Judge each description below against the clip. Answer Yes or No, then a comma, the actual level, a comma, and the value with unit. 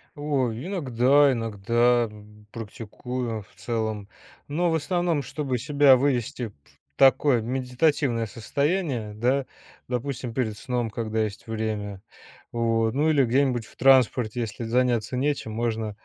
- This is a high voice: No, low, 125 Hz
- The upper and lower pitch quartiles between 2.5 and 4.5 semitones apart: Yes, average, 3.7 semitones